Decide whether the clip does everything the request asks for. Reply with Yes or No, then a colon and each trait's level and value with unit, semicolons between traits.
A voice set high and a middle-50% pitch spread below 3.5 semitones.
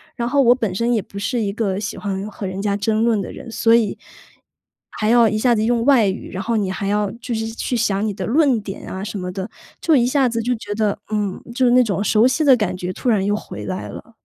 Yes: high, 215 Hz; average, 3.1 semitones